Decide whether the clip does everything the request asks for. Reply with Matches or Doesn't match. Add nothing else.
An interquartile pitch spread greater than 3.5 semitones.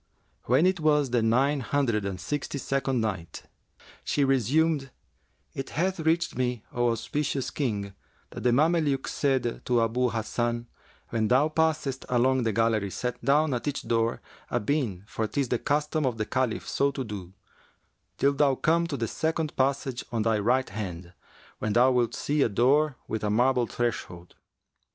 Matches